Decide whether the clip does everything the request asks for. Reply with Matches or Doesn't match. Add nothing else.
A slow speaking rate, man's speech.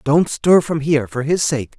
Doesn't match